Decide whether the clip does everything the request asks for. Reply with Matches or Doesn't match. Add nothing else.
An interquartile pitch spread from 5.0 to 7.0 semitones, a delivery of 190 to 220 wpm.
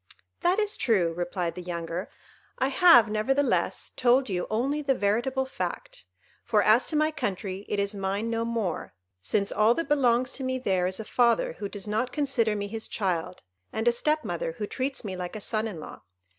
Matches